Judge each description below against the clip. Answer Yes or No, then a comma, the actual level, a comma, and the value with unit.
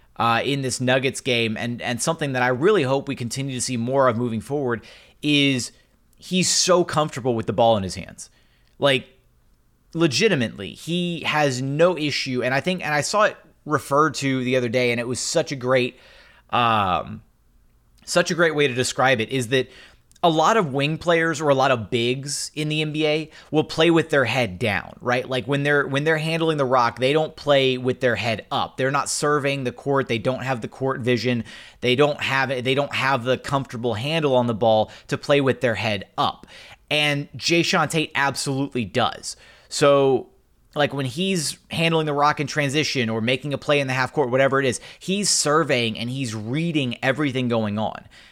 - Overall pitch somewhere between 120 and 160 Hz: Yes, low, 135 Hz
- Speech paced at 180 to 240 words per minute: Yes, average, 200 wpm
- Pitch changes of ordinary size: Yes, average, 3.4 semitones